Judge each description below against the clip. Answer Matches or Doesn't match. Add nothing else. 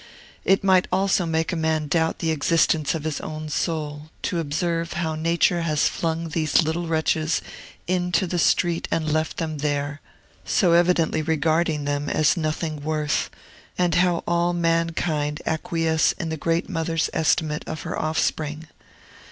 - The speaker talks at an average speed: Matches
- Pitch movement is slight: Matches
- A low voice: Doesn't match